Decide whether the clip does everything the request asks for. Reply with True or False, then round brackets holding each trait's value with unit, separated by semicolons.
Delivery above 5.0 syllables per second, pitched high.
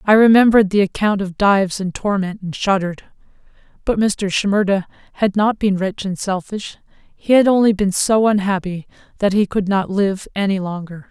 True (5.2 syllables/s; 200 Hz)